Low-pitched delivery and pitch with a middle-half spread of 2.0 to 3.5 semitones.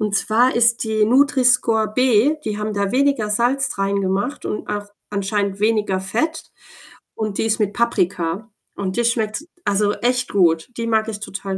No: high, 215 Hz; average, 2.9 semitones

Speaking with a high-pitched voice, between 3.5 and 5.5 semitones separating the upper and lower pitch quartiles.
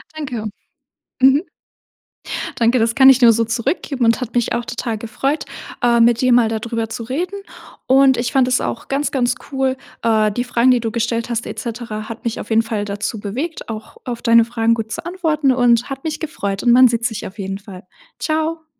No: high, 235 Hz; average, 2.8 semitones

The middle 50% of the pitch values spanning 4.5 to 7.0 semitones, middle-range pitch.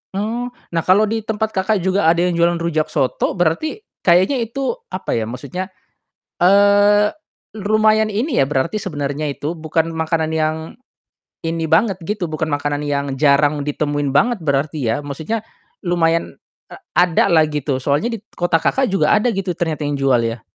Yes: wide, 5.5 semitones; medium, 165 Hz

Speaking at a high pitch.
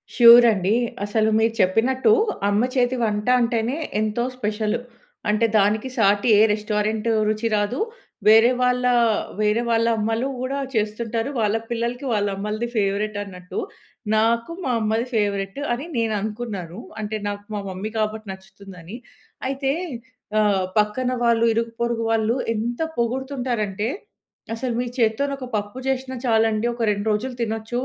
Yes: high, 220 Hz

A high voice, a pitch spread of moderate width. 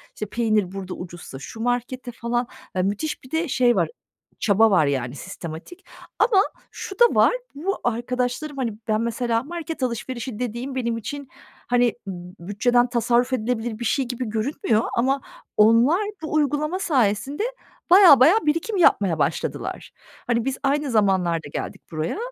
Yes: high, 240 Hz; average, 4.6 semitones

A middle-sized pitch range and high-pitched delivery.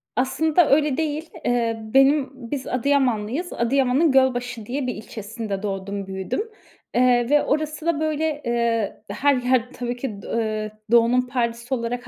Yes: average, 3.8 semitones; very high, 250 Hz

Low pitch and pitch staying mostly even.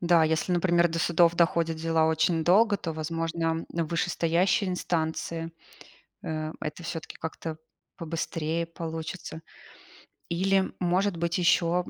No: medium, 165 Hz; narrow, 1.3 semitones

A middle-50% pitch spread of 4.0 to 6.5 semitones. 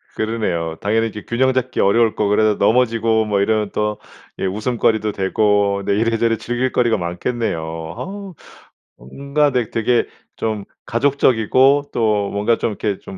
No: average, 3.0 semitones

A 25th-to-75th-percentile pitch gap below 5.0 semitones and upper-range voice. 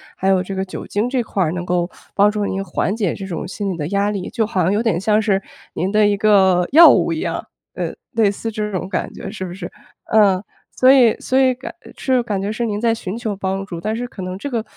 Yes: average, 2.8 semitones; high, 205 Hz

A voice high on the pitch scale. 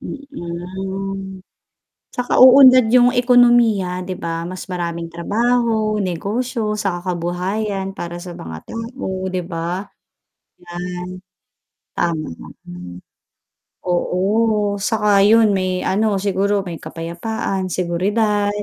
Yes: high, 195 Hz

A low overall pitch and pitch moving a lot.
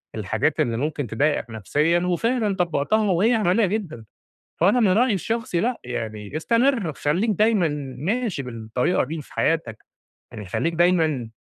No: medium, 170 Hz; wide, 7.8 semitones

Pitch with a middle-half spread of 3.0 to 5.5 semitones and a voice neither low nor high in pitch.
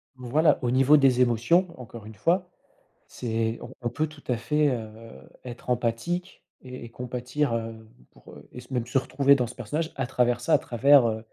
No: average, 3.3 semitones; low, 125 Hz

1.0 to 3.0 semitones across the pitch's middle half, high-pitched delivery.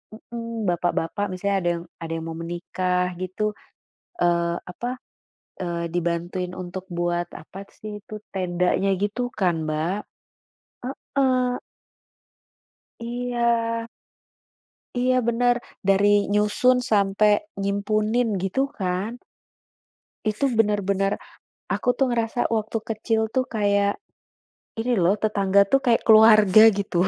No: average, 4.1 semitones; high, 205 Hz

